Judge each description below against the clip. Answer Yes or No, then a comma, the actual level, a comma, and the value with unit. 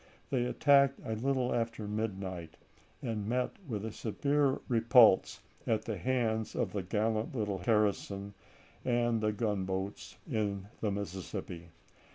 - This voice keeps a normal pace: No, slow, 130 wpm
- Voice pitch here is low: Yes, low, 110 Hz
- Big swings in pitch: No, average, 3.1 semitones